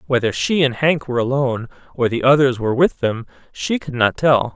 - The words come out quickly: Yes, fast, 210 wpm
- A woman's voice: No, male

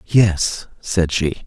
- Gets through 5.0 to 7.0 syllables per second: No, 2.6 syllables/s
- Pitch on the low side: Yes, very low, 90 Hz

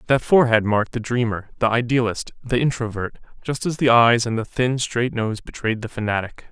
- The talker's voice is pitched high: No, low, 115 Hz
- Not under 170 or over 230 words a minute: Yes, average, 195 wpm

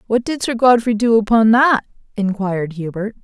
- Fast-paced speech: No, average, 165 wpm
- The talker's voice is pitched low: No, high, 220 Hz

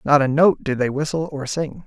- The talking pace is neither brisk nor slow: No, fast, 260 wpm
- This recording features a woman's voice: No, male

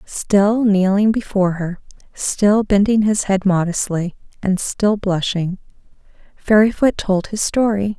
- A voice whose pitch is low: No, high, 200 Hz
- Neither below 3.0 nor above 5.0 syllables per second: Yes, 4.0 syllables/s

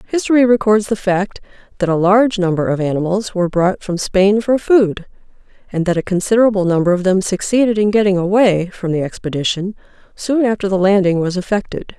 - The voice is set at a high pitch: Yes, high, 195 Hz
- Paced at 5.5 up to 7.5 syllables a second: Yes, 5.8 syllables/s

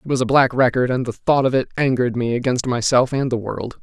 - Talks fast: Yes, fast, 265 wpm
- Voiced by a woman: No, male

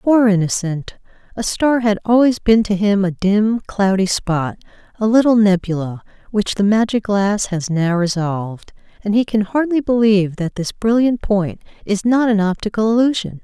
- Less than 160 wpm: No, average, 165 wpm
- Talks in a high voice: Yes, high, 205 Hz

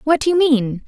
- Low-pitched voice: No, very high, 280 Hz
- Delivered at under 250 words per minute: No, fast, 275 wpm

